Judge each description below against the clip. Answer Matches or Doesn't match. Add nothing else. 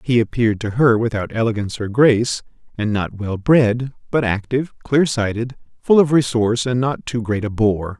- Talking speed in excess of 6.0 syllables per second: Doesn't match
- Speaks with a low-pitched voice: Matches